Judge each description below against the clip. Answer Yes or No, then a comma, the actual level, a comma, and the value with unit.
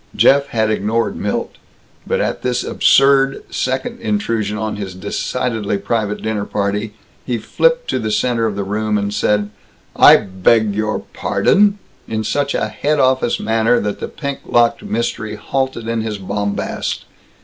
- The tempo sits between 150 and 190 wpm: Yes, average, 155 wpm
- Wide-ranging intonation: No, average, 3.3 semitones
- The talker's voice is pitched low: Yes, low, 110 Hz